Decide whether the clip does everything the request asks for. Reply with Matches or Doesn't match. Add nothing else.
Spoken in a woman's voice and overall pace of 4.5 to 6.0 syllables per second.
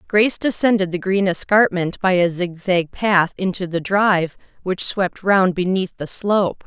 Matches